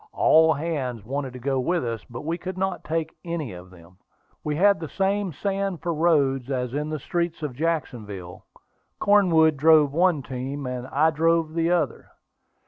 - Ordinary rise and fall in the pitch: Yes, average, 4.6 semitones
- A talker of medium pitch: Yes, medium, 155 Hz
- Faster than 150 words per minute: Yes, average, 175 wpm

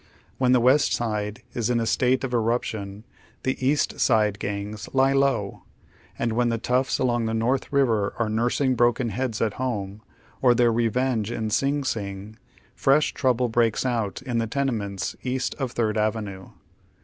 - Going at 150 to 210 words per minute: Yes, average, 175 wpm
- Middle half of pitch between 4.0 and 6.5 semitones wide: No, average, 3.1 semitones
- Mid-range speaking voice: No, low, 120 Hz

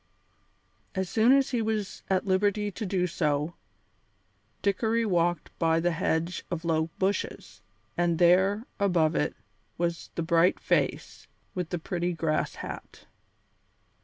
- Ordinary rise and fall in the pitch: Yes, average, 3.2 semitones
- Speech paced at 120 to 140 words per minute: Yes, slow, 135 wpm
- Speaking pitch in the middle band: Yes, medium, 180 Hz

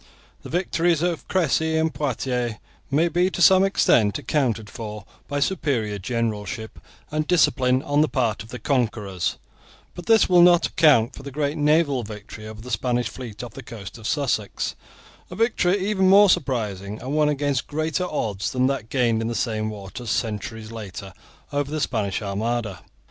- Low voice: Yes, low, 125 Hz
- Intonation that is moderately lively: No, wide, 6.1 semitones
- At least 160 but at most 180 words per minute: Yes, average, 175 wpm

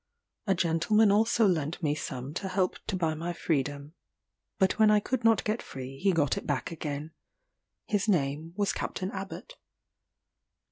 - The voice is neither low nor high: Yes, medium, 175 Hz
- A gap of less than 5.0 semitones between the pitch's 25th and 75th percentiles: No, wide, 5.5 semitones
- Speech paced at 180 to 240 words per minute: No, average, 160 wpm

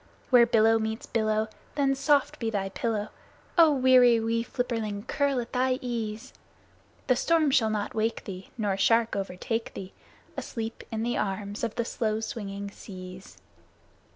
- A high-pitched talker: Yes, high, 225 Hz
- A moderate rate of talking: Yes, average, 155 wpm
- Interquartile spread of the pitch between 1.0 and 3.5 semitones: Yes, average, 2.9 semitones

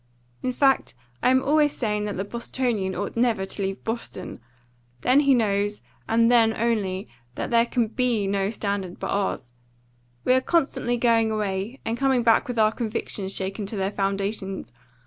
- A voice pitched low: No, high, 220 Hz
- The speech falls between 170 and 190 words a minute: Yes, average, 175 wpm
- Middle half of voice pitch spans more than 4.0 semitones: No, average, 3.5 semitones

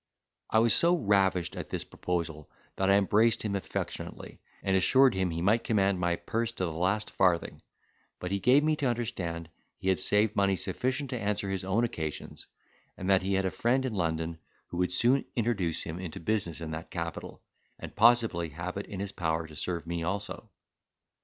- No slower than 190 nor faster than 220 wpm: Yes, average, 195 wpm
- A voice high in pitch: No, very low, 95 Hz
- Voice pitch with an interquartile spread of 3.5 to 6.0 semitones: Yes, average, 4.6 semitones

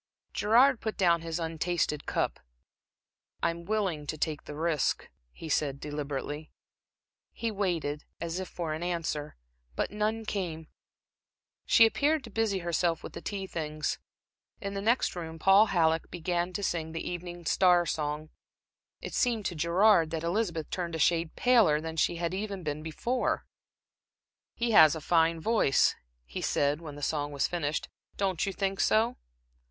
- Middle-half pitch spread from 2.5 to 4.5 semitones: Yes, average, 4.1 semitones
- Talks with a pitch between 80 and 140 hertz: No, medium, 170 Hz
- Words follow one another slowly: No, average, 160 wpm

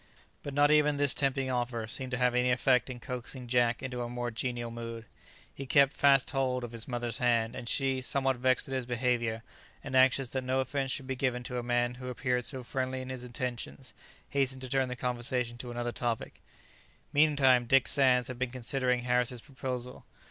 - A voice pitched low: Yes, low, 125 Hz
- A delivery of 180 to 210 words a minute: Yes, average, 200 wpm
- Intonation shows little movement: Yes, narrow, 1.5 semitones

